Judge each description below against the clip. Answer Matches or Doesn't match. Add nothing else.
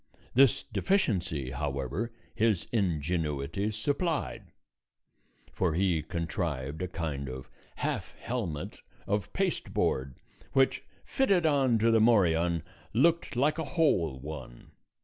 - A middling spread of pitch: Doesn't match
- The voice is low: Matches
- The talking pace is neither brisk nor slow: Doesn't match